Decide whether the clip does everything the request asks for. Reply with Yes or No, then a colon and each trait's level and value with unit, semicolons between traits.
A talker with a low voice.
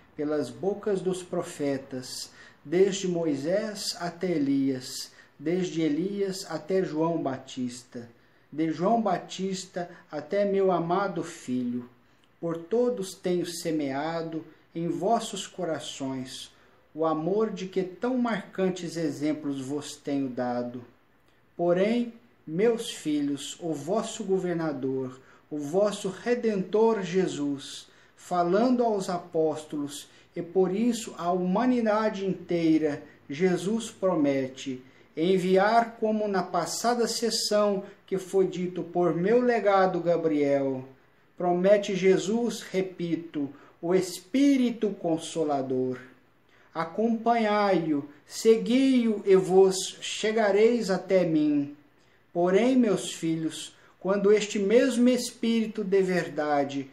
No: medium, 175 Hz